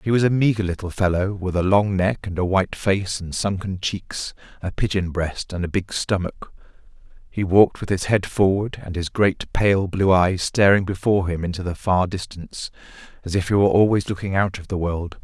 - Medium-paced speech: No, fast, 210 wpm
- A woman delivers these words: No, male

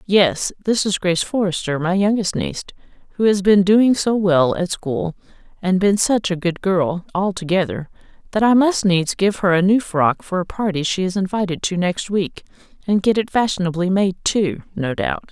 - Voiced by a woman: Yes, female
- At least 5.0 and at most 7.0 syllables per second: No, 4.8 syllables/s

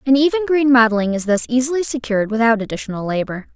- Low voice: No, high, 240 Hz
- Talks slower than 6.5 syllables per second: No, 6.6 syllables/s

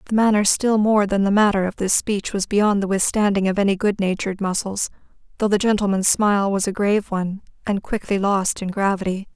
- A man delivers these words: No, female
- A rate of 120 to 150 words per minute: No, average, 200 wpm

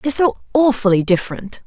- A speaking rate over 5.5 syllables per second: Yes, 6.0 syllables/s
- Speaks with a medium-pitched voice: No, high, 230 Hz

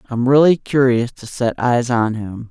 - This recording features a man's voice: Yes, male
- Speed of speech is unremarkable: Yes, average, 190 wpm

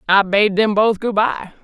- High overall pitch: Yes, high, 205 Hz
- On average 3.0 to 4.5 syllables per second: Yes, 4.3 syllables/s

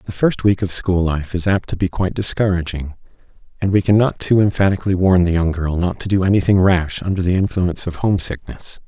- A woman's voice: No, male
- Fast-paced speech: Yes, fast, 215 wpm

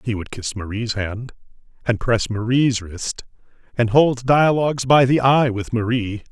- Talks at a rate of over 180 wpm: No, average, 160 wpm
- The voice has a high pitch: No, low, 120 Hz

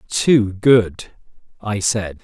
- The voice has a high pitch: No, low, 105 Hz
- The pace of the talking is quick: No, slow, 105 wpm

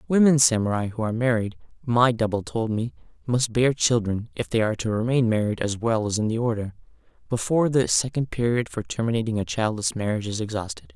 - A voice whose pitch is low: Yes, low, 115 Hz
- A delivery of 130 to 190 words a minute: Yes, average, 180 wpm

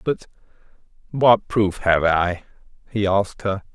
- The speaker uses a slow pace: Yes, slow, 130 wpm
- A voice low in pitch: Yes, low, 100 Hz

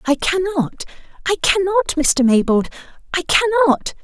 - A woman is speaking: Yes, female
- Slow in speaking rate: Yes, slow, 105 wpm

